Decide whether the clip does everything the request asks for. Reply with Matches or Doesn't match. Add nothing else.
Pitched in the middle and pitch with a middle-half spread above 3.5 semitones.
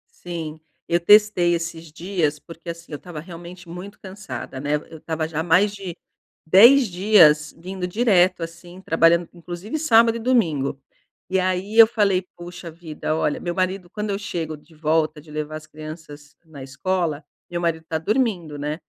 Doesn't match